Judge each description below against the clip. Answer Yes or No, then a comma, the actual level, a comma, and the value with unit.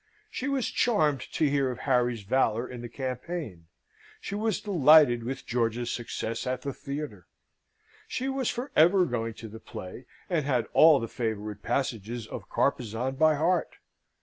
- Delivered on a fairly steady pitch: No, wide, 5.4 semitones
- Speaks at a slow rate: No, average, 160 wpm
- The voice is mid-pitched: No, low, 130 Hz